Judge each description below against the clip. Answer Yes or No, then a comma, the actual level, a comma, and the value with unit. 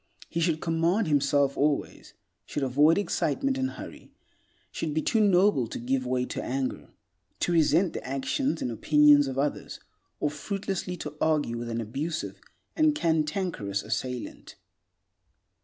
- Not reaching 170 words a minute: Yes, average, 140 wpm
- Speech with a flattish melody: No, average, 5.0 semitones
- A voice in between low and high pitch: Yes, medium, 150 Hz